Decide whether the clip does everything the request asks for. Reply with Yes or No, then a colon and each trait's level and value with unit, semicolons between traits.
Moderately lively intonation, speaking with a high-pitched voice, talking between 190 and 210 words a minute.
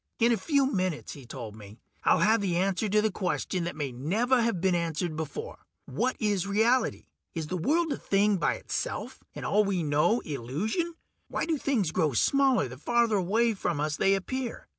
No: wide, 6.6 semitones; high, 195 Hz; average, 195 wpm